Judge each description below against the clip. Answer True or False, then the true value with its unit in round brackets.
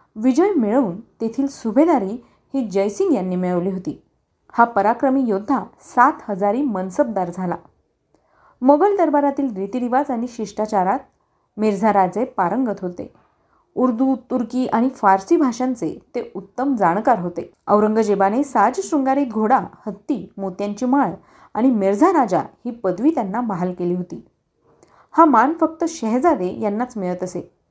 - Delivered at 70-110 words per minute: False (125 wpm)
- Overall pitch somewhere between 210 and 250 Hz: True (235 Hz)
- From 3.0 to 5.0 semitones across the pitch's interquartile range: False (5.5 semitones)